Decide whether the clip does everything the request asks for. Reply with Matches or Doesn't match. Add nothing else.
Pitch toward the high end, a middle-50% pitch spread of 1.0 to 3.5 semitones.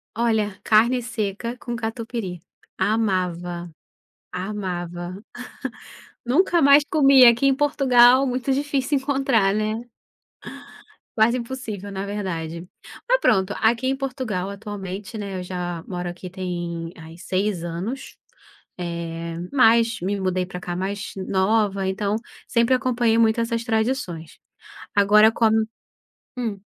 Doesn't match